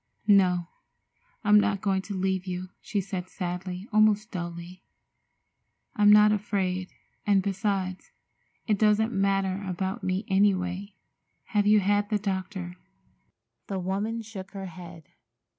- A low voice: No, high, 195 Hz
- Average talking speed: No, slow, 130 wpm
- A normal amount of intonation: No, narrow, 2.0 semitones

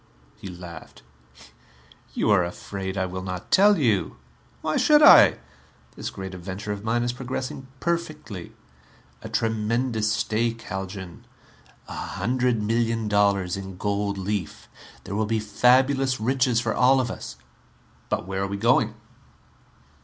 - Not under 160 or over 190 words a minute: No, average, 140 wpm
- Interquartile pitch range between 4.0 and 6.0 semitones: Yes, average, 4.3 semitones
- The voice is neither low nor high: No, low, 110 Hz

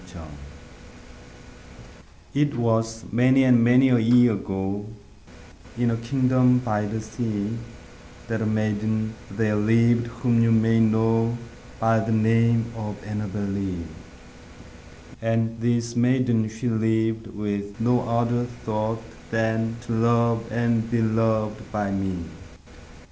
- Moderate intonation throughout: No, narrow, 1.5 semitones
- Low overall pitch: Yes, low, 115 Hz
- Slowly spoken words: Yes, slow, 120 wpm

